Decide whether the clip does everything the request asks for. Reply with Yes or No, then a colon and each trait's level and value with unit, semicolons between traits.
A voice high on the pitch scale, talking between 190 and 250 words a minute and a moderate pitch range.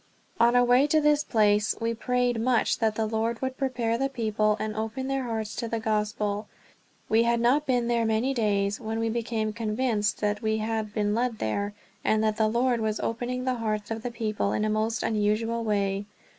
No: high, 225 Hz; fast, 205 wpm; narrow, 2.1 semitones